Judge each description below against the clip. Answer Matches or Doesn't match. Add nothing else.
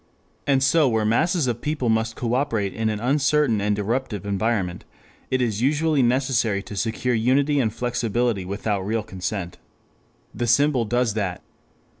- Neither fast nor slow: Matches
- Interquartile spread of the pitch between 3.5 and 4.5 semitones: Matches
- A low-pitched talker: Matches